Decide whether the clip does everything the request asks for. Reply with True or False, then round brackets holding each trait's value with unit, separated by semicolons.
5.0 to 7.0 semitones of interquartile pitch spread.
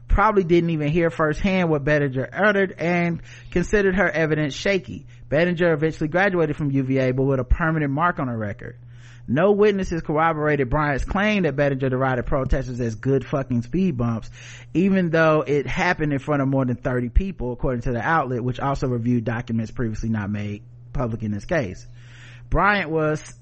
True (5.4 semitones)